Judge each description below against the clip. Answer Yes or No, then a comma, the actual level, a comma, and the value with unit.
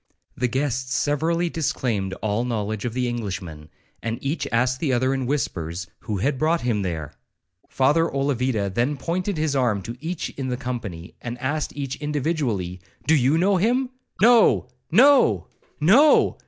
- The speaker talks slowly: No, average, 155 wpm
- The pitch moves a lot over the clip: Yes, wide, 5.8 semitones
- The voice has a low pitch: Yes, low, 130 Hz